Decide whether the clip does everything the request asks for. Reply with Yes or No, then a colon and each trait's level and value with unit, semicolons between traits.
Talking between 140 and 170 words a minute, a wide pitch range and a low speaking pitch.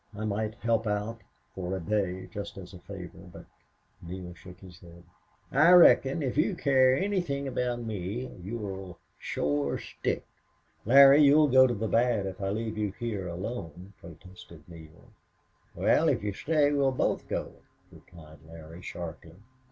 Yes: average, 160 wpm; wide, 6.0 semitones; low, 105 Hz